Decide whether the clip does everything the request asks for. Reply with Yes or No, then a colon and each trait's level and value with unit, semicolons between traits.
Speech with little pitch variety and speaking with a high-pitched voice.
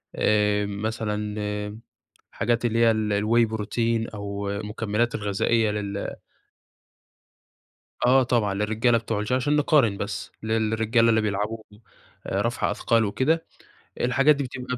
No: narrow, 2.1 semitones; low, 110 Hz